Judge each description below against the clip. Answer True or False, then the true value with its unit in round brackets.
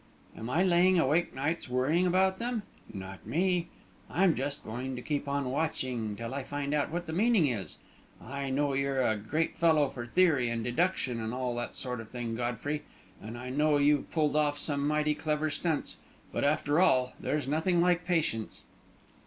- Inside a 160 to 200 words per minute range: True (185 wpm)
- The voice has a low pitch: False (145 Hz)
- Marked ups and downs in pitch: False (4.5 semitones)